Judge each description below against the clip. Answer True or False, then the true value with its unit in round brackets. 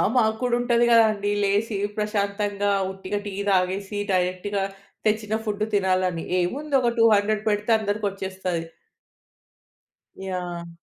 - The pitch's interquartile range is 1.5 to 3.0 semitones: True (2.4 semitones)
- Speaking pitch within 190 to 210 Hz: True (205 Hz)